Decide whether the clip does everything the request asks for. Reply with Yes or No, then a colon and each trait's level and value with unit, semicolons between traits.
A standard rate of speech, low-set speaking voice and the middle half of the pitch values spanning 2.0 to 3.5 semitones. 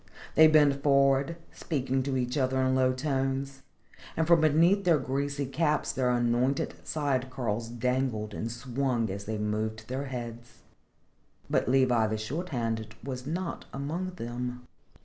Yes: average, 150 wpm; low, 130 Hz; average, 2.9 semitones